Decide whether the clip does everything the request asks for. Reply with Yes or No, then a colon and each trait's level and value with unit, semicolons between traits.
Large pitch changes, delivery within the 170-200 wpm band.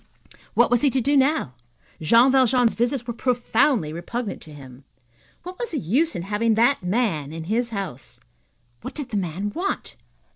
Yes: wide, 6.8 semitones; average, 175 wpm